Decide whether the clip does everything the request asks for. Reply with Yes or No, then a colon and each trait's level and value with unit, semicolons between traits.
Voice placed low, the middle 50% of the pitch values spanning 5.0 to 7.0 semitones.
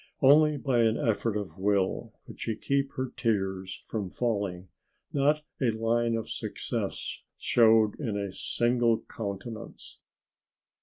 No: low, 115 Hz; average, 3.3 semitones